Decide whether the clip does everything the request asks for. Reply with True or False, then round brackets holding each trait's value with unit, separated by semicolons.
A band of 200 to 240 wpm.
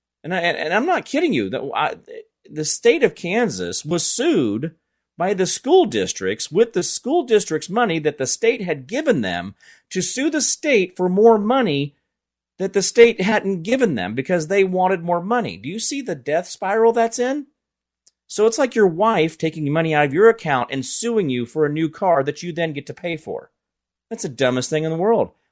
True (205 wpm)